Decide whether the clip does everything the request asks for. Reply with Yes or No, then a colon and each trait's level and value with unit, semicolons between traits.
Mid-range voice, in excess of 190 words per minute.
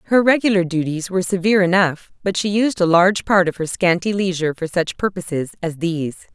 Yes: medium, 180 Hz; average, 200 wpm